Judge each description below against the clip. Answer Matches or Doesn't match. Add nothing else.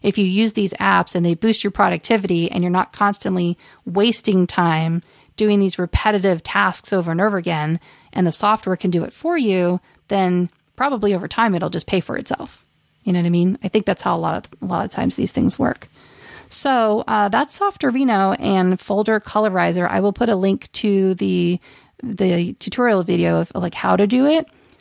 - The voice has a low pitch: Doesn't match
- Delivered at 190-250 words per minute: Matches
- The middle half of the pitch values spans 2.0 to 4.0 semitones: Matches